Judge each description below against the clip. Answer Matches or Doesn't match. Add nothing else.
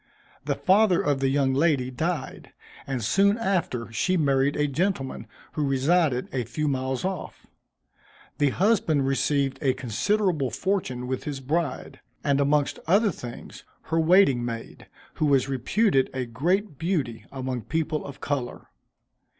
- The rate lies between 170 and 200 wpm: Doesn't match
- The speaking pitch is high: Doesn't match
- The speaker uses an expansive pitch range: Doesn't match